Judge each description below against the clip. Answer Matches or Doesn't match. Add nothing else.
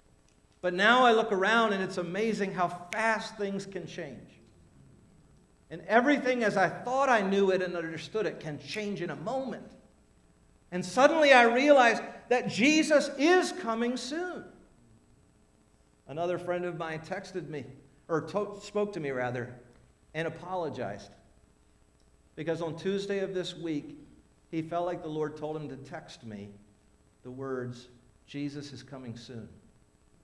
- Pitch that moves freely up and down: Matches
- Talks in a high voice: Doesn't match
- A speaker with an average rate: Matches